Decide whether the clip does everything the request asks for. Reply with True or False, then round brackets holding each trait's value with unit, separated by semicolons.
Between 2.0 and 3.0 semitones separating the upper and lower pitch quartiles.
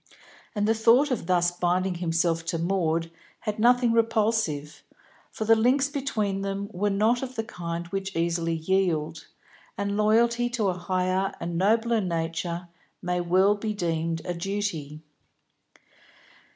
False (4.5 semitones)